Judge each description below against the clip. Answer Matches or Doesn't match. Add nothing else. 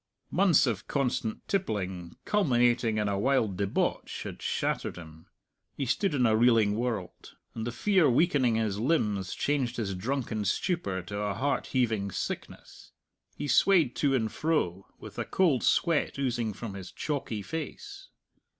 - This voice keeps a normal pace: Matches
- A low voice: Matches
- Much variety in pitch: Matches